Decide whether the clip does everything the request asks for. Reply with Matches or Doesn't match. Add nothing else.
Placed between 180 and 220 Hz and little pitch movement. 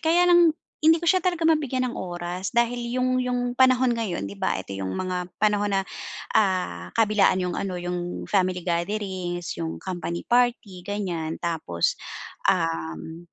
Doesn't match